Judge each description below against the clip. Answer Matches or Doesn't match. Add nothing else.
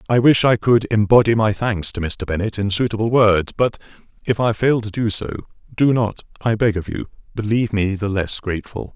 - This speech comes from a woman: Doesn't match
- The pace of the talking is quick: Matches